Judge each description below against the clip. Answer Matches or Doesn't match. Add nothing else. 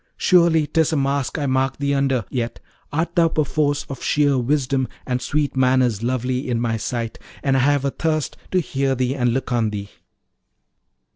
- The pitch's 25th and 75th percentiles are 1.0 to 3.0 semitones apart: Matches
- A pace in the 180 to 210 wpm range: Matches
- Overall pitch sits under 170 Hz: Matches